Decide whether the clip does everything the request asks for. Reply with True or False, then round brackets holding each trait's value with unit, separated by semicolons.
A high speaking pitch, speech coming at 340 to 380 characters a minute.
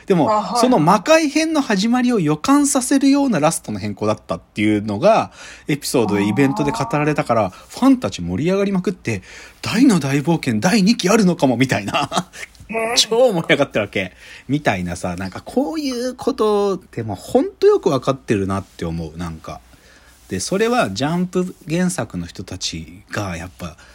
False (155 Hz; 365 characters per minute)